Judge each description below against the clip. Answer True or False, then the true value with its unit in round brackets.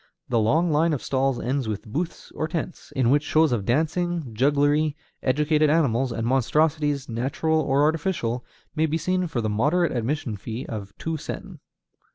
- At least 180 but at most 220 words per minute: False (170 wpm)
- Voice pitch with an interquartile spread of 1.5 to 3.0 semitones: False (4.6 semitones)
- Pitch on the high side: False (145 Hz)